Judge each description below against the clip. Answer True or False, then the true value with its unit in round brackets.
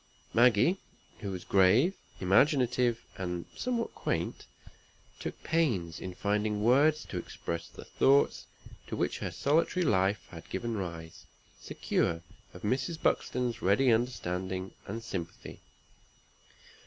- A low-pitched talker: True (110 Hz)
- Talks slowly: True (115 wpm)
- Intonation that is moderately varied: False (6.0 semitones)